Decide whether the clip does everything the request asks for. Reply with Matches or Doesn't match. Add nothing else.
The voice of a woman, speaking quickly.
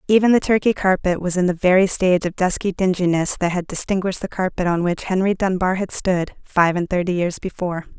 Matches